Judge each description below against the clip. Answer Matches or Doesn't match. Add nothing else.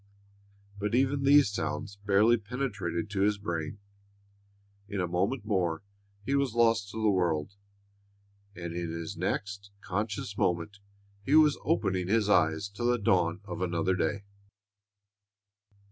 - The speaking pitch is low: Matches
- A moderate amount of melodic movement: Matches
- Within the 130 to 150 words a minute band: Matches